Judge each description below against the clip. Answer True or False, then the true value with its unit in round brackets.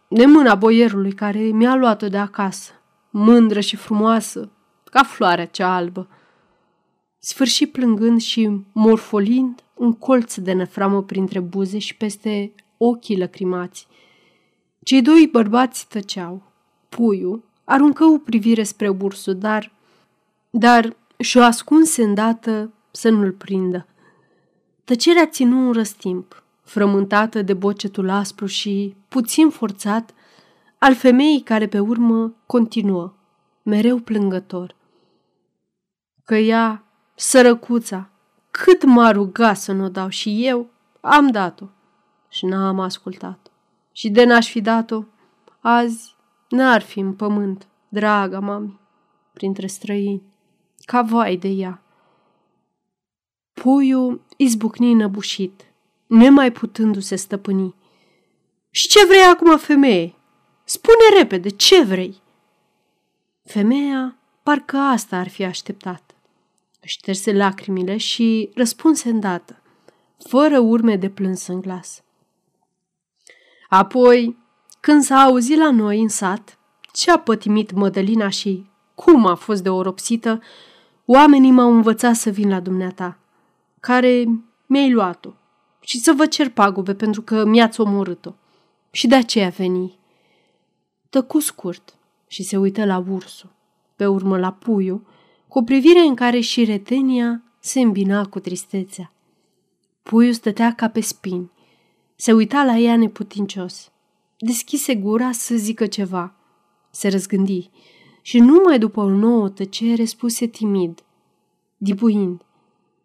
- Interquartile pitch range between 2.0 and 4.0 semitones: True (3.6 semitones)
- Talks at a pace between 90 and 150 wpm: True (120 wpm)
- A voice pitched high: True (215 Hz)